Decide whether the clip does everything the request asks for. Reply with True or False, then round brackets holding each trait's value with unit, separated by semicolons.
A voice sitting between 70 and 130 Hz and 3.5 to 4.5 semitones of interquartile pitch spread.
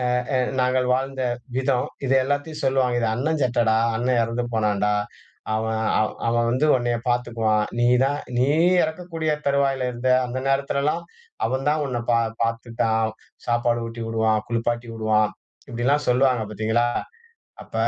False (120 Hz; 2.9 semitones)